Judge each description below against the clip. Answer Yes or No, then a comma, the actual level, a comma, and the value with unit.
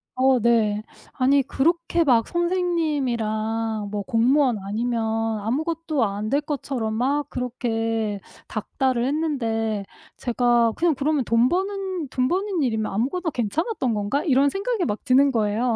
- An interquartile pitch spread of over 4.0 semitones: Yes, average, 5.2 semitones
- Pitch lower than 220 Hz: No, very high, 255 Hz